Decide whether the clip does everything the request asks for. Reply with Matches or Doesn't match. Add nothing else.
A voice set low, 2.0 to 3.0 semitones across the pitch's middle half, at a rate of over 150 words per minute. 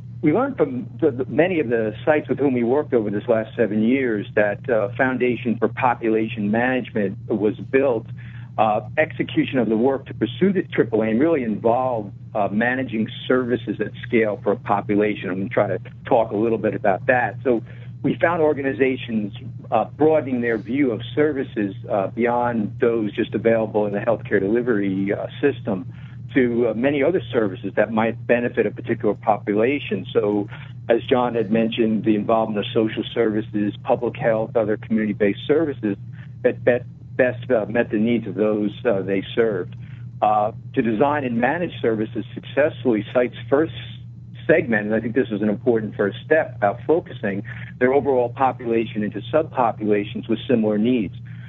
Matches